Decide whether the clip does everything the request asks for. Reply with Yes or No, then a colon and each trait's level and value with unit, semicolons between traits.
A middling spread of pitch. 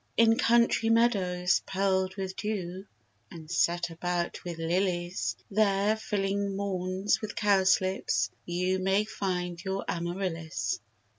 No: narrow, 2.2 semitones